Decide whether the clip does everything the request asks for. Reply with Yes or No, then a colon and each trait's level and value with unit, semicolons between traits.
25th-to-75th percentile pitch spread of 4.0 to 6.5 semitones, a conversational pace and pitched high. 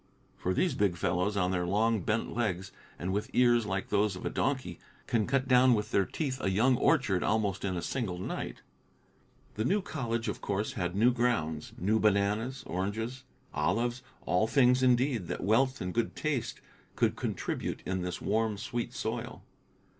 No: average, 4.5 semitones; average, 175 wpm; low, 110 Hz